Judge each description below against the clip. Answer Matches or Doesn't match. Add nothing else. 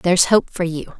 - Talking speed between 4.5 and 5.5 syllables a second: Matches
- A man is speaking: Doesn't match